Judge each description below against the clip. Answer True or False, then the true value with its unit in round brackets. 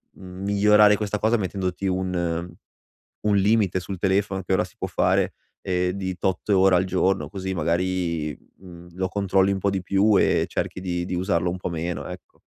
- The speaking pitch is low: True (95 Hz)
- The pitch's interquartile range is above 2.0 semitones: False (1.7 semitones)